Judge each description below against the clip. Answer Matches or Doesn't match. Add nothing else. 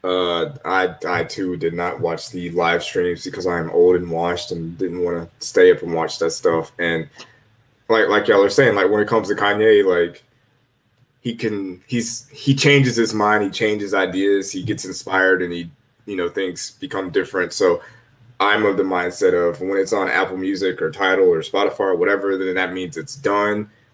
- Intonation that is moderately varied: Doesn't match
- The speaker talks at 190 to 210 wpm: Matches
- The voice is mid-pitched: Doesn't match